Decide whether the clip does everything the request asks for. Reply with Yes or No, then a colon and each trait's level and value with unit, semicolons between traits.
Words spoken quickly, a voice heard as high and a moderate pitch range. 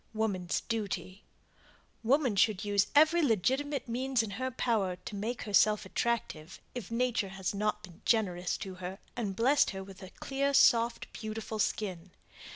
No: average, 155 wpm; high, 215 Hz; average, 4.1 semitones